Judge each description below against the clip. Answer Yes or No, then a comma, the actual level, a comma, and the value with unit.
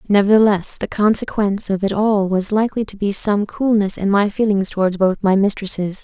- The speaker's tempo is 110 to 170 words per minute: No, average, 190 wpm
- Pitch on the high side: Yes, high, 200 Hz